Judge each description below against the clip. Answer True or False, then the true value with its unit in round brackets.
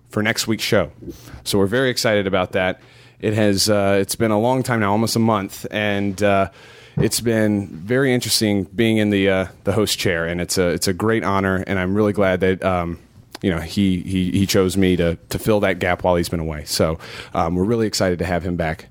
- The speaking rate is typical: False (225 wpm)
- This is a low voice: True (100 Hz)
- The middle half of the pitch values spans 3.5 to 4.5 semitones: False (2.8 semitones)